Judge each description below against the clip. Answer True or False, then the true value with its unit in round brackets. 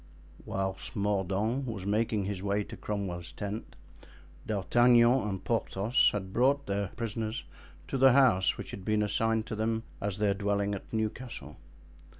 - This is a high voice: False (105 Hz)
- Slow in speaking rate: False (150 wpm)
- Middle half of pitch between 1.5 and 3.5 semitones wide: True (2.6 semitones)